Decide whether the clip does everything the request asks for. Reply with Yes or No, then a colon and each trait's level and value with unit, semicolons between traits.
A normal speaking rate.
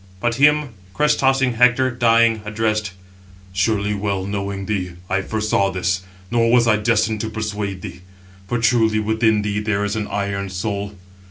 Yes: average, 160 wpm